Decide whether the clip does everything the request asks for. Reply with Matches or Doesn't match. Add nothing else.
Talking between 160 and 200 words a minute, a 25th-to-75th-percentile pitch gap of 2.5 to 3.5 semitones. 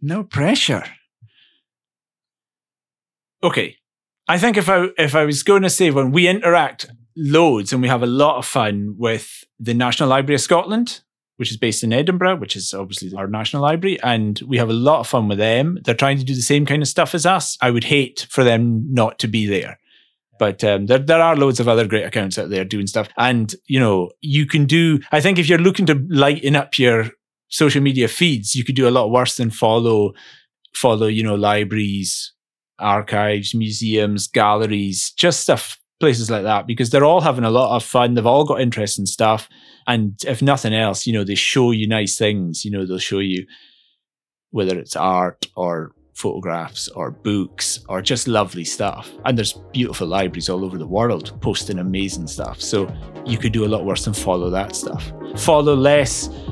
Doesn't match